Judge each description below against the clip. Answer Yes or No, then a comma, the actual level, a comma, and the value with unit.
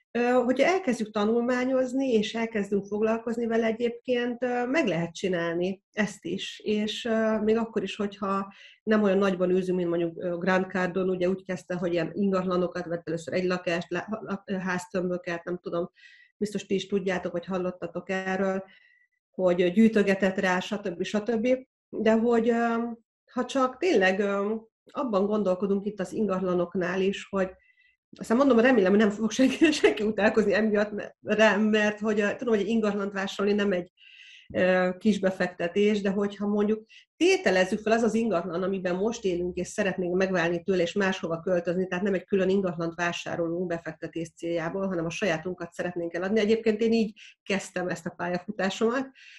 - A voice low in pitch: No, high, 200 Hz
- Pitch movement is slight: No, average, 3.5 semitones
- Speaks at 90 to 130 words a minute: No, average, 150 wpm